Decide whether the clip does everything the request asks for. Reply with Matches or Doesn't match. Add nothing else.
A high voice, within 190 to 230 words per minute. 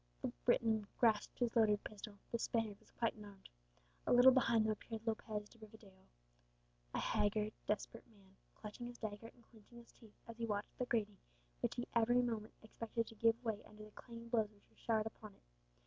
Matches